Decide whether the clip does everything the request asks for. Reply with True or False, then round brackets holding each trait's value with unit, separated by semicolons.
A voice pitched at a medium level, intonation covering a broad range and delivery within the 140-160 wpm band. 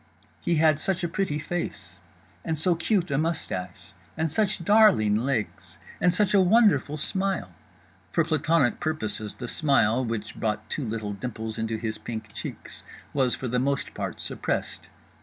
True (145 Hz; 7.4 semitones; 150 wpm)